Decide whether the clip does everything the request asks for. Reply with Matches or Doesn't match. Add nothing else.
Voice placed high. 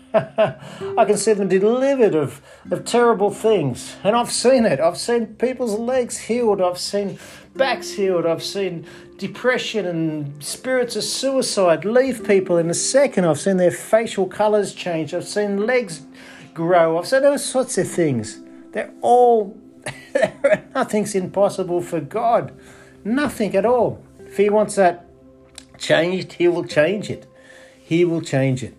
Matches